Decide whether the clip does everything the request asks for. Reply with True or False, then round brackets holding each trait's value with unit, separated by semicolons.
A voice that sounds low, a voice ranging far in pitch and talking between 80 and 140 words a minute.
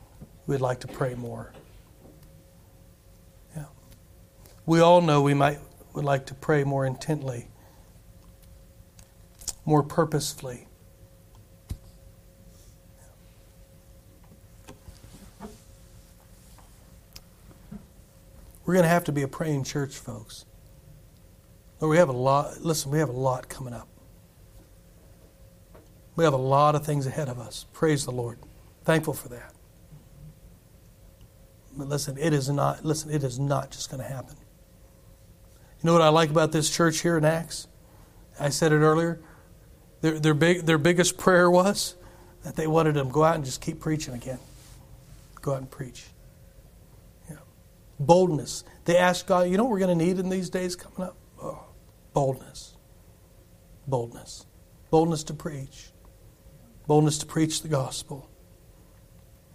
True (130 Hz; 8.9 semitones; 135 wpm)